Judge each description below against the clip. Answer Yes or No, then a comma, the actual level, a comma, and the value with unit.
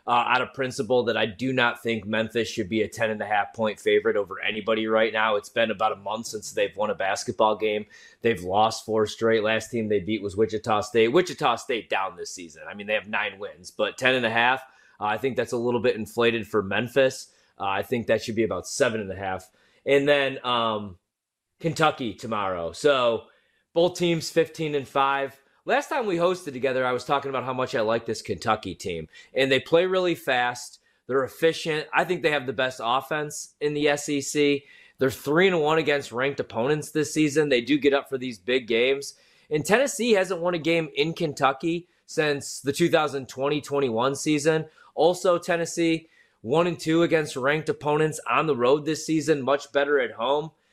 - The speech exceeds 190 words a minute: Yes, fast, 205 wpm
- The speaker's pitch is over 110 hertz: Yes, low, 135 Hz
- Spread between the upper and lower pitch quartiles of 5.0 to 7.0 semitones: Yes, wide, 5.4 semitones